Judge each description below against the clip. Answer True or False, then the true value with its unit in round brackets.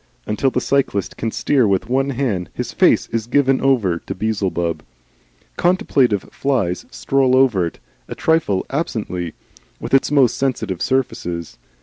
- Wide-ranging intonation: True (6.3 semitones)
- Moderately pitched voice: False (115 Hz)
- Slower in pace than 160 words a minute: True (140 wpm)